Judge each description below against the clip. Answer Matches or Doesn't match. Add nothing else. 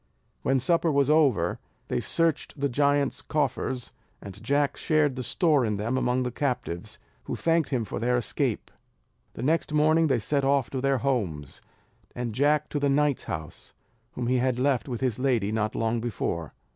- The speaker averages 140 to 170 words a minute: Doesn't match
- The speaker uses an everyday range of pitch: Matches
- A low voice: Matches